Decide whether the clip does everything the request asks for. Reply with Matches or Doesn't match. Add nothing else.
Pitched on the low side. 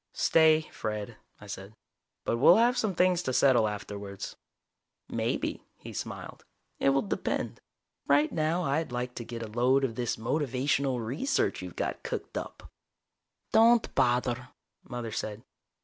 Matches